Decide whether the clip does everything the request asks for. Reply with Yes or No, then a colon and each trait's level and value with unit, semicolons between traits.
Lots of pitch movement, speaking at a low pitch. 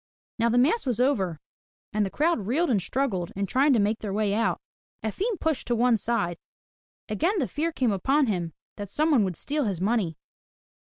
No: wide, 5.8 semitones; high, 230 Hz